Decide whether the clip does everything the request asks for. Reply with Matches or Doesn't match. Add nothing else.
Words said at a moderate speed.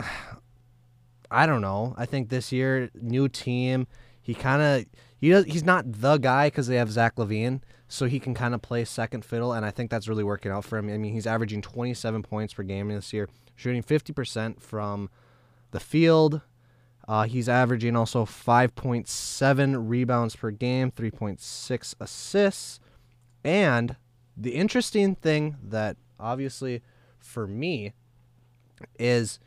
Matches